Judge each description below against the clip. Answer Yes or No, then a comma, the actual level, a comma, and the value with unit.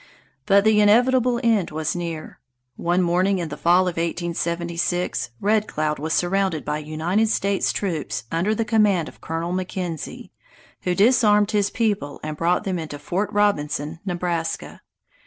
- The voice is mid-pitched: Yes, medium, 180 Hz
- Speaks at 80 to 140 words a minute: No, average, 150 wpm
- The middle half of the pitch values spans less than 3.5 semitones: No, average, 3.9 semitones